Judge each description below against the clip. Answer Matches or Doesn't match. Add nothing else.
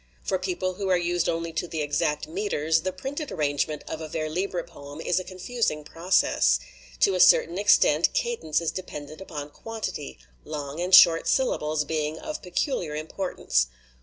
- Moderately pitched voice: Matches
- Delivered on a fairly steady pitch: Doesn't match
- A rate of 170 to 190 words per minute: Matches